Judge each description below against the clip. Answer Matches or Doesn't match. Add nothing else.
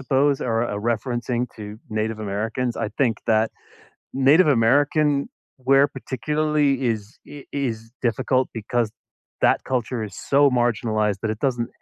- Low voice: Matches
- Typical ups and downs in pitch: Matches